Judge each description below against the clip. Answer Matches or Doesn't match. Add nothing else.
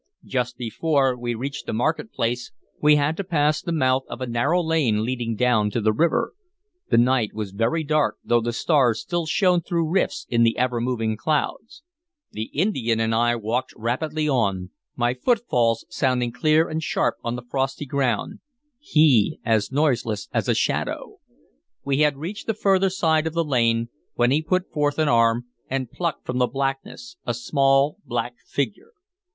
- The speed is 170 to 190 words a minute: Matches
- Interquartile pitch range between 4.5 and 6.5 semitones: Matches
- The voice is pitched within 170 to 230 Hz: Doesn't match